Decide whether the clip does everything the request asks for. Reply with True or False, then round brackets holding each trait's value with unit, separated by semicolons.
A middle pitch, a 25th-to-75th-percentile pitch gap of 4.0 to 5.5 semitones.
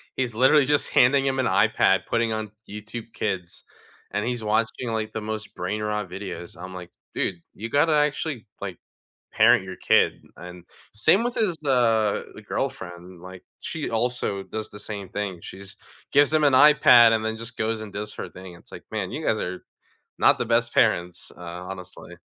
False (110 Hz; 4.4 semitones)